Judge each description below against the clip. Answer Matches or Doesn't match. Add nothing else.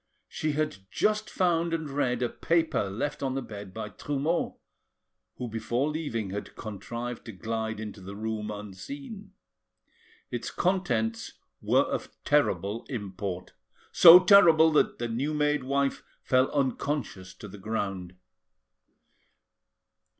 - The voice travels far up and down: Matches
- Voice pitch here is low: Matches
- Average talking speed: Doesn't match